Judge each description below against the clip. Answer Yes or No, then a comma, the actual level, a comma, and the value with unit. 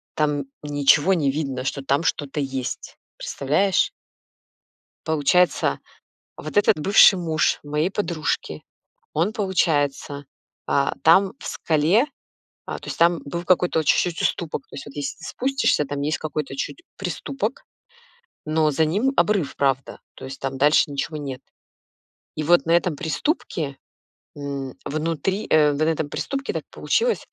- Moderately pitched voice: Yes, medium, 155 Hz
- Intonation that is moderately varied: Yes, average, 3.9 semitones